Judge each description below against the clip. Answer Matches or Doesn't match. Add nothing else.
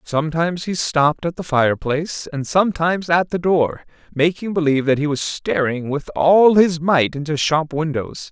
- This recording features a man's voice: Matches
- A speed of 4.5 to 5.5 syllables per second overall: Matches